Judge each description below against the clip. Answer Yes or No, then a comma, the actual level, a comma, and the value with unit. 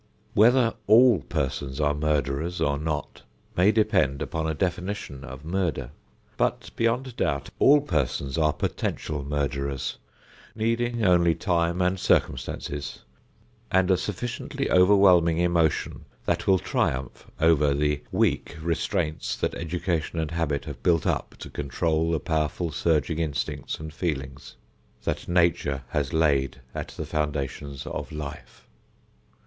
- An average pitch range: Yes, average, 4.2 semitones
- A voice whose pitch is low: Yes, very low, 80 Hz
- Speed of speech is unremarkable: No, slow, 130 wpm